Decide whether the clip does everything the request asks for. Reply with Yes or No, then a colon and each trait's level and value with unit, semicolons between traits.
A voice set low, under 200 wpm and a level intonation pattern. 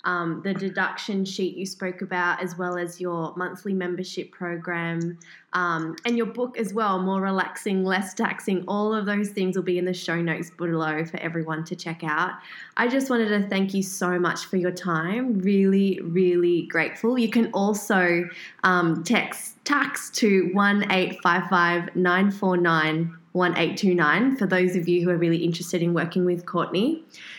No: medium, 180 Hz; average, 160 wpm; narrow, 2.2 semitones